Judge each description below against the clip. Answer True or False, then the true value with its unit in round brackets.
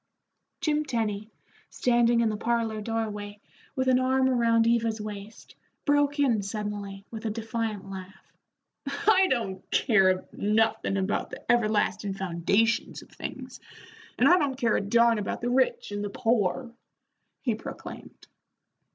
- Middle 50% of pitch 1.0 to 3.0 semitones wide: True (2.7 semitones)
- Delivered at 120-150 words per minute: True (140 wpm)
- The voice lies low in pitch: False (225 Hz)